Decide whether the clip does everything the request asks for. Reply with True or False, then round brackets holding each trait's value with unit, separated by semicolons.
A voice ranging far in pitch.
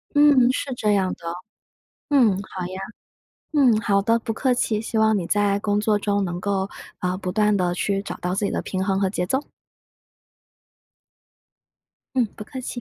False (3.0 semitones)